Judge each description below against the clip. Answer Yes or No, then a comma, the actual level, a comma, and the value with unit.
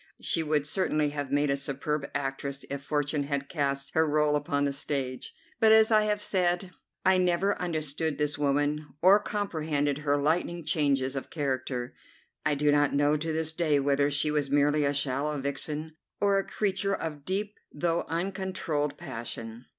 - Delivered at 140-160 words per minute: No, average, 170 wpm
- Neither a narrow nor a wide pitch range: Yes, average, 3.1 semitones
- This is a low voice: No, medium, 150 Hz